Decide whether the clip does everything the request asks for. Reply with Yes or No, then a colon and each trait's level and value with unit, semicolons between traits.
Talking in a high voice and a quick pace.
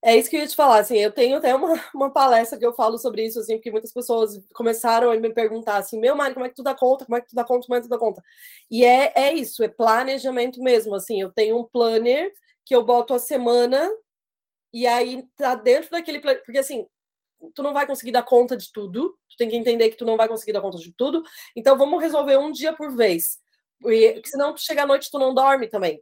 Yes: high, 245 Hz; fast, 255 wpm